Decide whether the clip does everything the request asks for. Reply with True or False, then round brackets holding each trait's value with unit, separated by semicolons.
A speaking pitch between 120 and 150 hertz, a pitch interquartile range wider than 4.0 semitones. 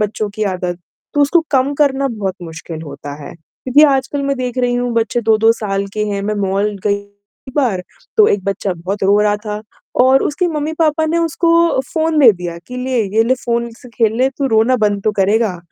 False (230 Hz; 5.1 semitones)